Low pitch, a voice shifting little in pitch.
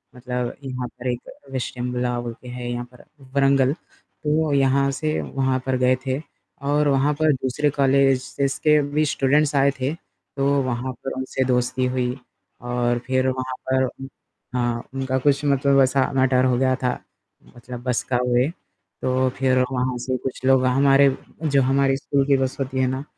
Yes: low, 130 Hz; narrow, 1.5 semitones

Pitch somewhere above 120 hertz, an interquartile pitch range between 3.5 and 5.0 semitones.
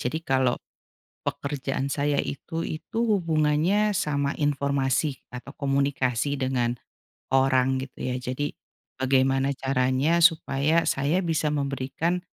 No: medium, 140 Hz; narrow, 2.6 semitones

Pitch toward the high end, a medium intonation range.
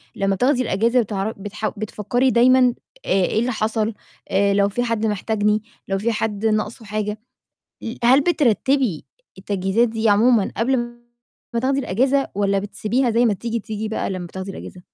Yes: high, 220 Hz; average, 3.1 semitones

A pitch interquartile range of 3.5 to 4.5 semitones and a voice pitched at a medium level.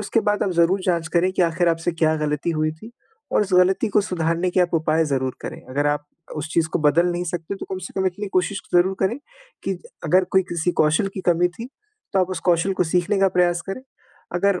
No: average, 2.7 semitones; medium, 175 Hz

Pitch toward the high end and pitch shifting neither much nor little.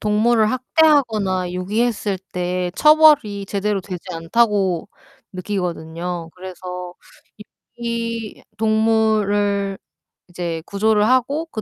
Yes: high, 205 Hz; average, 3.8 semitones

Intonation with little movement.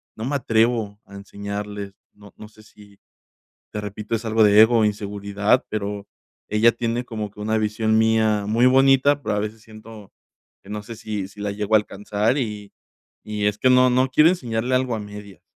Yes: narrow, 1.9 semitones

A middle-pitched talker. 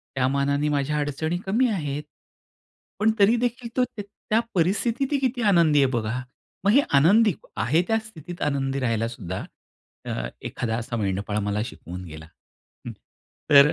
Yes: medium, 145 Hz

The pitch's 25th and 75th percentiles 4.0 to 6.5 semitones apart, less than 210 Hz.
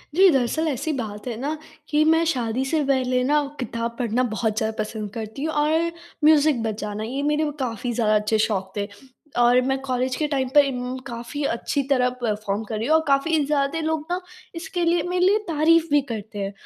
No: average, 5.1 semitones; very high, 260 Hz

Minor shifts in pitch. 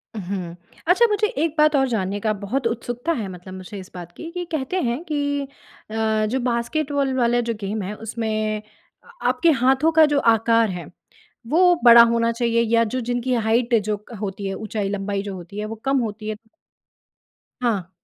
No: average, 4.5 semitones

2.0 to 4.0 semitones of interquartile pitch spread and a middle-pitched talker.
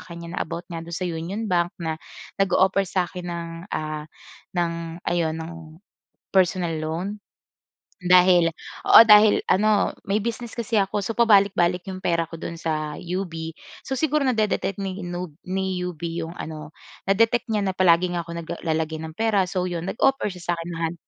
Yes: average, 2.9 semitones; medium, 180 Hz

